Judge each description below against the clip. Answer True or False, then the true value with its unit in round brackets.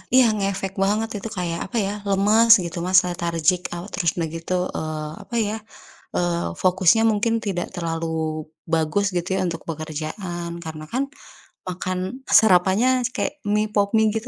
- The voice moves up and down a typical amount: True (3.5 semitones)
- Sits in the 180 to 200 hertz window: True (185 Hz)